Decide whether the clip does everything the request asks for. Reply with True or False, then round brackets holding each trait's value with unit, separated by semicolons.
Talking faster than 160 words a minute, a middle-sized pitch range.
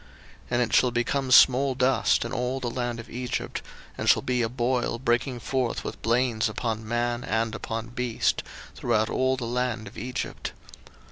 False (180 wpm; 1.6 semitones)